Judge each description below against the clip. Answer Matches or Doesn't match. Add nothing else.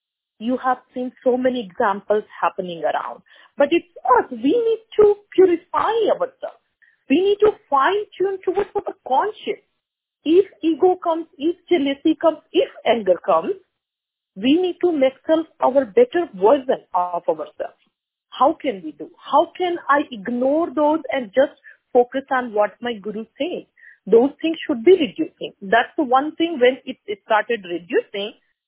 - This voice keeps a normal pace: Matches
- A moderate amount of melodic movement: Doesn't match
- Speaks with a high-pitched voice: Matches